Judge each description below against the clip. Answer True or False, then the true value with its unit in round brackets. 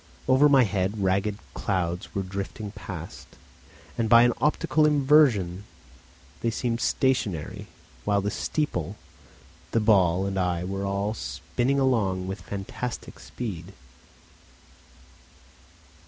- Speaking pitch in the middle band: False (100 Hz)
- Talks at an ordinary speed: False (110 wpm)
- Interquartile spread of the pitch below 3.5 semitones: False (4.5 semitones)